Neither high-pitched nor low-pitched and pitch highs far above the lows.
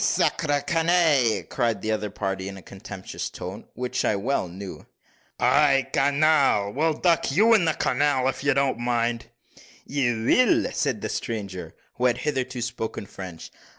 No: low, 125 Hz; wide, 5.7 semitones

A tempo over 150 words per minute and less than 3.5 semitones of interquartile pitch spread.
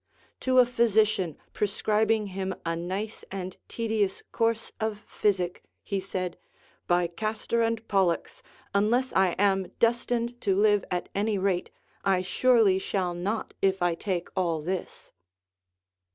No: slow, 135 wpm; average, 3.1 semitones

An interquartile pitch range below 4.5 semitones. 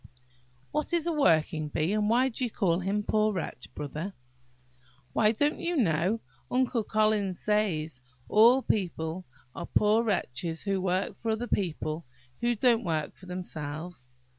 No: wide, 5.6 semitones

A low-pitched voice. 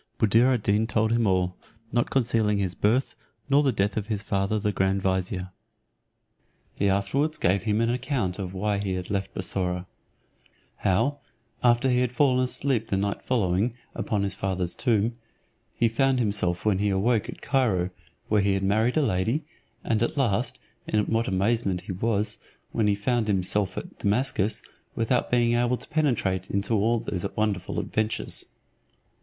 Yes: low, 105 Hz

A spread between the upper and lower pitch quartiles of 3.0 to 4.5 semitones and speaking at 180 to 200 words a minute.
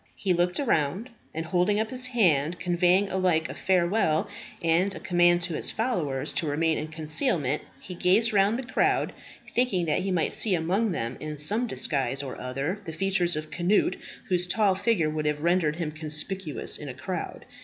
Yes: average, 4.0 semitones; average, 185 wpm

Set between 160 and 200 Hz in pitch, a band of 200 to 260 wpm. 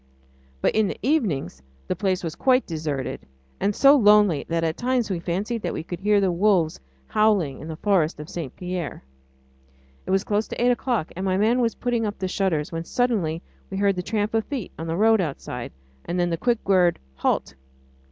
Yes: high, 190 Hz; fast, 205 wpm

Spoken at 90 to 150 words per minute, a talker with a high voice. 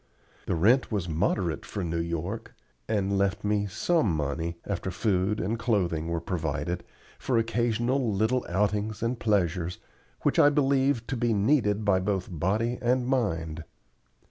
No: average, 145 wpm; low, 100 Hz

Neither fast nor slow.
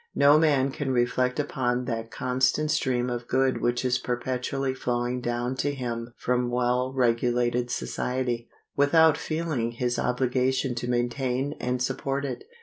Yes: average, 145 wpm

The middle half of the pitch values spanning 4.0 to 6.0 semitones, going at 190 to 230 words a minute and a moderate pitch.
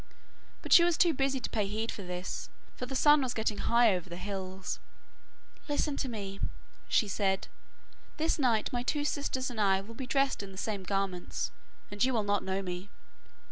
No: average, 5.2 semitones; average, 195 wpm; high, 215 Hz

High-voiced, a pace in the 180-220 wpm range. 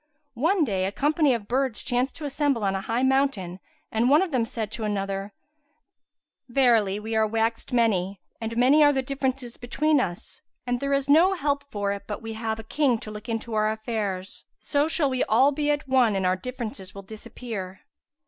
Yes: high, 235 Hz; average, 200 wpm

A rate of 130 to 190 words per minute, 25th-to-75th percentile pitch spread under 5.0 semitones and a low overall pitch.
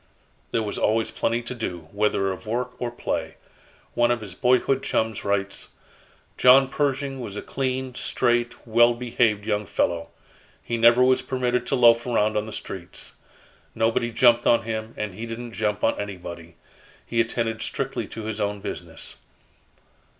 Yes: average, 160 wpm; narrow, 2.6 semitones; low, 115 Hz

